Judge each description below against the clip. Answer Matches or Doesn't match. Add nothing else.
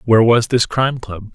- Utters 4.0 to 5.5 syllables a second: Doesn't match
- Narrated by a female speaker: Doesn't match